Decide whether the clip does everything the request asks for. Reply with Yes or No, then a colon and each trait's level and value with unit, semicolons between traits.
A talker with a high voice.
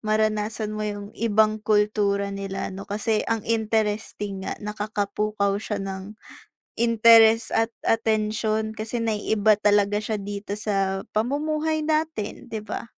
Yes: high, 215 Hz